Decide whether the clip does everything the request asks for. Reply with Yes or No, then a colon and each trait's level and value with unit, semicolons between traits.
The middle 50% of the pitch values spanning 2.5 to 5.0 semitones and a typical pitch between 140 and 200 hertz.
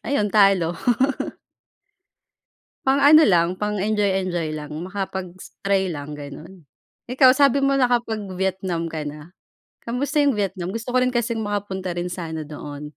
No: wide, 5.6 semitones; high, 190 Hz